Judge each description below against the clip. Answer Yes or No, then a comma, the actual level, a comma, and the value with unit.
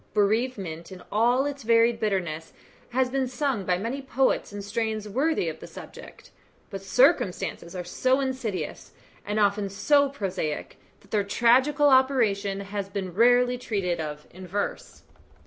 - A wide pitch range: No, average, 4.8 semitones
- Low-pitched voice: No, high, 215 Hz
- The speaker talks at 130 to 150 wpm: Yes, average, 145 wpm